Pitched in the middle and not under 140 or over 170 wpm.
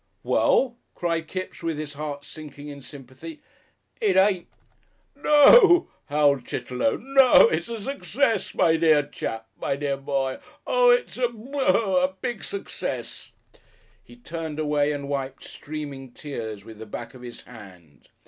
Yes: medium, 155 Hz; average, 155 wpm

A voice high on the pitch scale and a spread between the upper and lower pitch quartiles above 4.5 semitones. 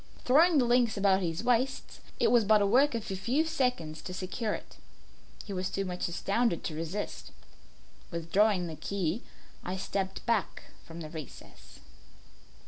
Yes: high, 200 Hz; average, 5.2 semitones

